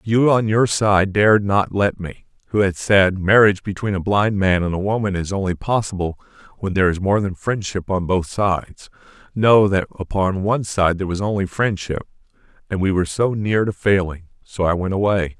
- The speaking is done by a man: Yes, male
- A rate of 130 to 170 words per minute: No, average, 200 wpm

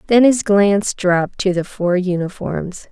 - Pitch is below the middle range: No, high, 190 Hz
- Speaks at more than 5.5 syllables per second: No, 4.4 syllables/s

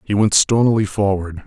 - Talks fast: No, average, 165 wpm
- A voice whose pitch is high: No, low, 100 Hz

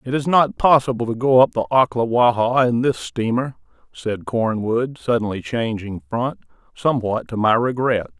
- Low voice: Yes, low, 120 Hz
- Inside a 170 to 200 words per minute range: No, average, 155 wpm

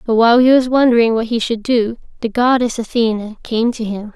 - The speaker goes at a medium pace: No, fast, 215 wpm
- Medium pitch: No, high, 230 Hz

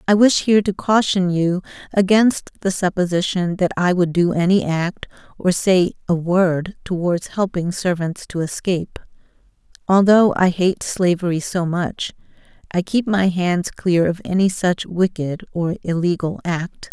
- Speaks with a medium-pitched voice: Yes, medium, 180 Hz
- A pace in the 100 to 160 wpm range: Yes, average, 150 wpm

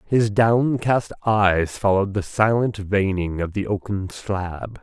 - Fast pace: No, slow, 135 wpm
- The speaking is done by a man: Yes, male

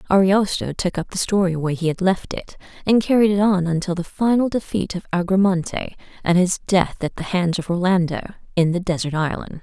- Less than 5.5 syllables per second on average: No, 5.6 syllables/s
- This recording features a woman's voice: Yes, female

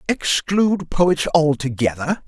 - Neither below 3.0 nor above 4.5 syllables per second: Yes, 4.0 syllables/s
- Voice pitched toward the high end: No, medium, 160 Hz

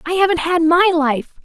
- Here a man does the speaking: No, female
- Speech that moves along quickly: Yes, fast, 210 wpm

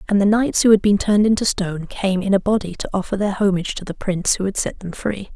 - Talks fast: Yes, fast, 280 wpm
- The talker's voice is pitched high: Yes, high, 200 Hz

